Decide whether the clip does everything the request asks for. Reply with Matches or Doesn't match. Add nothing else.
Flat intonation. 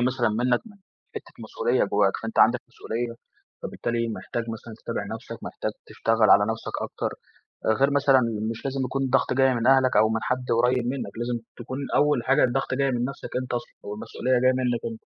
Matches